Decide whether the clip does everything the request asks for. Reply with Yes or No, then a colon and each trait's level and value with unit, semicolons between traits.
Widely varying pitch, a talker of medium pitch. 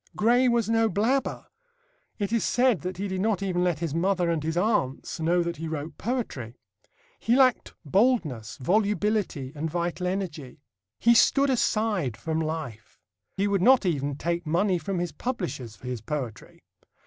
Yes: wide, 5.7 semitones; medium, 180 Hz